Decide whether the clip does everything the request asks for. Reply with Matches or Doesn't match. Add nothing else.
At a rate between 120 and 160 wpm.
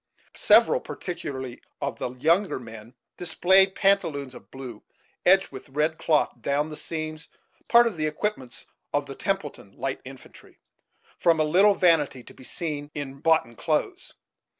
Matches